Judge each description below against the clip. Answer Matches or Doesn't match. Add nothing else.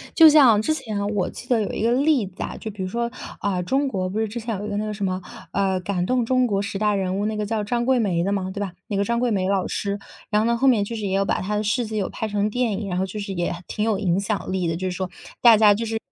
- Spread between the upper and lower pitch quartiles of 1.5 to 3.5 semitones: Matches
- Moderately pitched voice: Doesn't match